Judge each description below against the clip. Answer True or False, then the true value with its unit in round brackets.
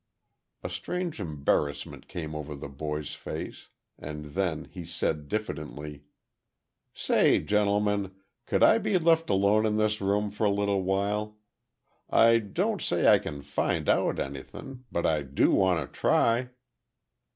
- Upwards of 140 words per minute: False (135 wpm)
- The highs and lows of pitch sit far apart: True (5.9 semitones)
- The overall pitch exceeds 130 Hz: False (95 Hz)